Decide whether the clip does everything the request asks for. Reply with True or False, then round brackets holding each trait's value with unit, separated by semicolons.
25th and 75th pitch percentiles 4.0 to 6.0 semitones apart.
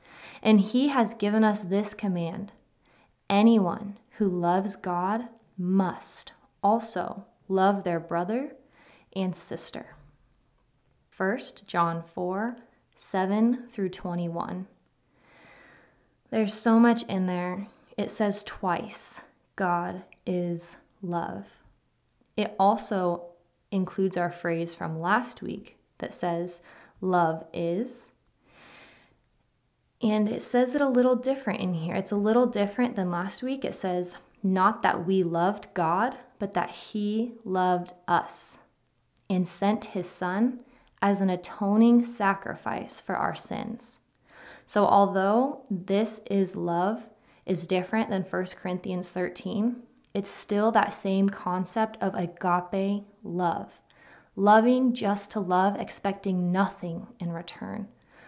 False (3.4 semitones)